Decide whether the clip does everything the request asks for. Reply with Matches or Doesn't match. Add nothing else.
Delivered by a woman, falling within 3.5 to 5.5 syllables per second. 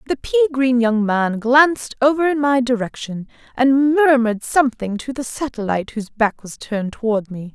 Matches